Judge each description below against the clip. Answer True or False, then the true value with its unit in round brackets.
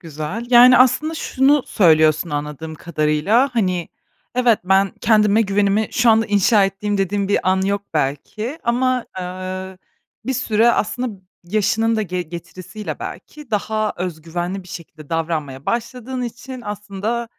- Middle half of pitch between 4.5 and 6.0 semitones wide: True (5.0 semitones)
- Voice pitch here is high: True (200 Hz)